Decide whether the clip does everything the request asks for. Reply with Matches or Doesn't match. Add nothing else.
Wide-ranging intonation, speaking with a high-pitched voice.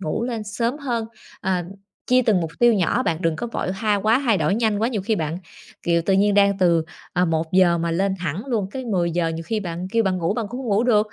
Doesn't match